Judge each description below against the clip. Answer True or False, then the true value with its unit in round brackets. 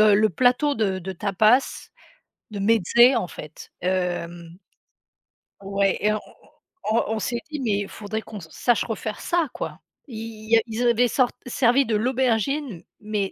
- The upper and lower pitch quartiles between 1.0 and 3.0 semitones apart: False (3.6 semitones)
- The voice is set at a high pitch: True (220 Hz)